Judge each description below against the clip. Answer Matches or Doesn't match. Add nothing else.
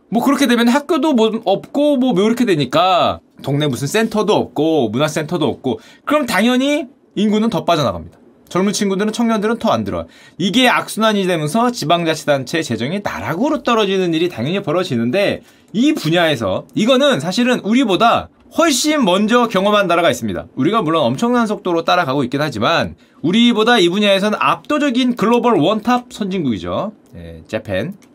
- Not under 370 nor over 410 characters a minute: Matches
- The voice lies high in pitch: Matches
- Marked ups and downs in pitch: Matches